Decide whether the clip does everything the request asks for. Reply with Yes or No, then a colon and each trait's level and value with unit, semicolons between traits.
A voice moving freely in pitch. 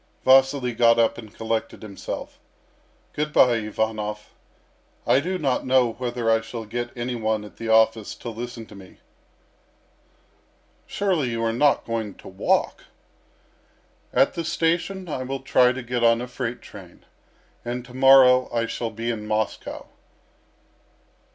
No: narrow, 2.6 semitones